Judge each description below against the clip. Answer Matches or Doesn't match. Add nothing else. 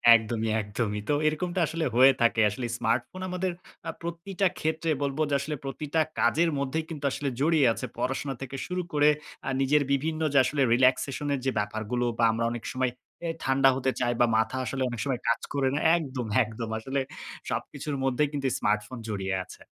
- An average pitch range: Matches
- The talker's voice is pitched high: Doesn't match